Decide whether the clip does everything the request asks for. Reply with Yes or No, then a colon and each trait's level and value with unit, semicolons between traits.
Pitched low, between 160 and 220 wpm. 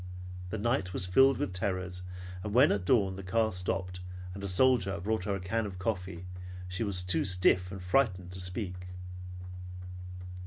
Yes: very low, 95 Hz; average, 170 wpm